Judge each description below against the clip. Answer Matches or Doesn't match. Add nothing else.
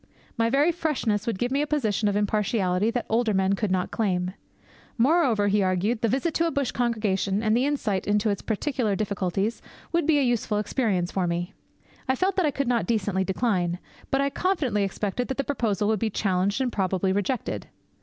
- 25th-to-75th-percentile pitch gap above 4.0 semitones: Matches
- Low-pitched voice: Doesn't match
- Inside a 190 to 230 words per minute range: Matches